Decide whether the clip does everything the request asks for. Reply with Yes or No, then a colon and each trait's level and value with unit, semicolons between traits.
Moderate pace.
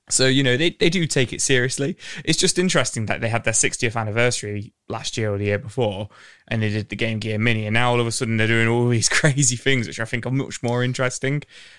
No: fast, 255 wpm